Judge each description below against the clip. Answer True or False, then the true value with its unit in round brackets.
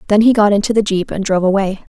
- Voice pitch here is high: True (205 Hz)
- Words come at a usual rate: False (275 wpm)